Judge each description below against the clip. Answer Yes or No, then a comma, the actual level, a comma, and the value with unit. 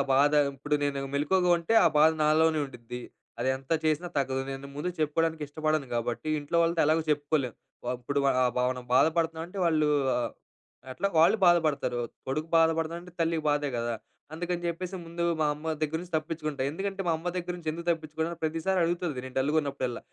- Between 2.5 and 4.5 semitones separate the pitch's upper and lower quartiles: Yes, average, 2.8 semitones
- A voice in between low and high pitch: Yes, medium, 155 Hz